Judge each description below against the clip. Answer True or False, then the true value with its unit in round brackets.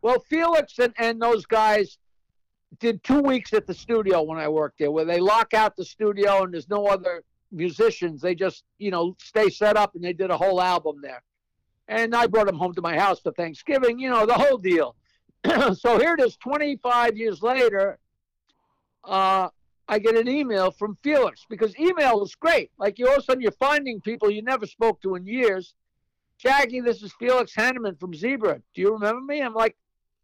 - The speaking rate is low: False (200 wpm)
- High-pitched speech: True (215 Hz)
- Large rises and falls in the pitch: False (4.7 semitones)